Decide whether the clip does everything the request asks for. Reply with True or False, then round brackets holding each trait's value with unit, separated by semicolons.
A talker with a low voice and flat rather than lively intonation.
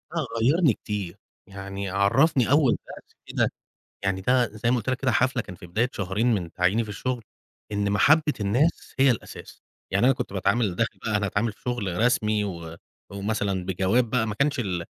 False (110 Hz; 4.3 semitones)